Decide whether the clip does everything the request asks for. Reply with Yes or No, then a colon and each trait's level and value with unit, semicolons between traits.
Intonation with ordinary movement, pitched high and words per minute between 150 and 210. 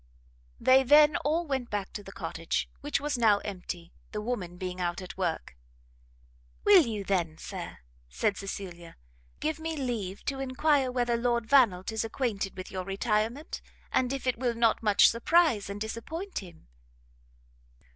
No: wide, 5.7 semitones; high, 225 Hz; average, 155 wpm